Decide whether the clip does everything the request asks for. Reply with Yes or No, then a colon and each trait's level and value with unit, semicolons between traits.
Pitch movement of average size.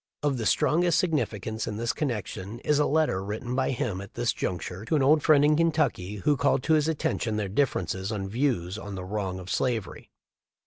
No: wide, 7.1 semitones